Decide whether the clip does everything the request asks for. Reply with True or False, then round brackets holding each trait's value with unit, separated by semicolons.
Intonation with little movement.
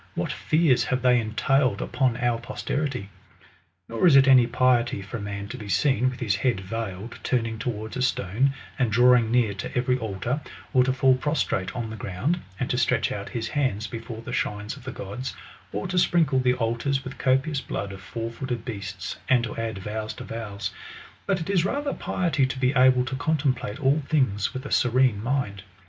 False (3.5 semitones)